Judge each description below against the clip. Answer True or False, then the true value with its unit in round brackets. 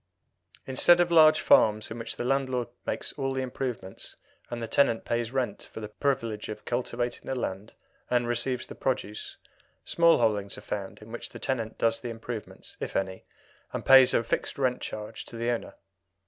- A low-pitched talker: True (120 Hz)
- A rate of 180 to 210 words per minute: True (185 wpm)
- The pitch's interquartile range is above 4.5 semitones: False (3.0 semitones)